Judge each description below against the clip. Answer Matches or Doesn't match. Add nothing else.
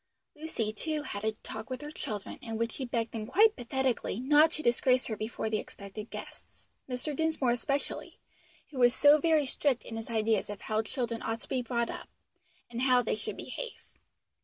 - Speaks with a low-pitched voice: Doesn't match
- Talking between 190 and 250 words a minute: Matches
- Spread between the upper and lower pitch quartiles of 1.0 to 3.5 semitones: Doesn't match